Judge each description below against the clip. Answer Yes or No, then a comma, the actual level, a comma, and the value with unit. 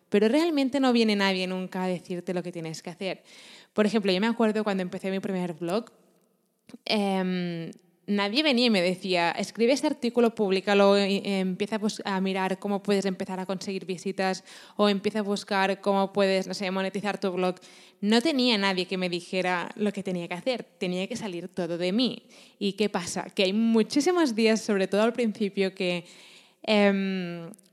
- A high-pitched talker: Yes, high, 195 Hz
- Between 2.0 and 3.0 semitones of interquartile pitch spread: Yes, narrow, 2.6 semitones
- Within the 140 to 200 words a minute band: Yes, average, 185 wpm